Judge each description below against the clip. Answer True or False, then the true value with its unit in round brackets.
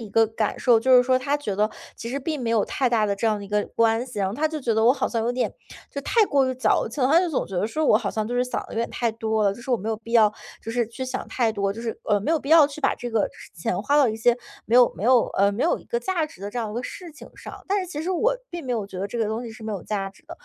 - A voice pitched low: False (235 Hz)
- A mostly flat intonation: False (3.8 semitones)